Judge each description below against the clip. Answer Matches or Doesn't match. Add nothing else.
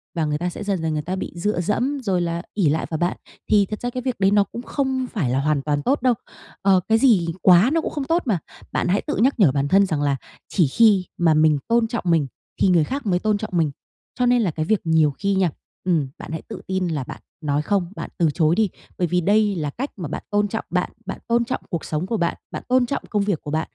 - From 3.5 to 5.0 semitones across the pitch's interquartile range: Doesn't match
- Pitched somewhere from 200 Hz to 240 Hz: Doesn't match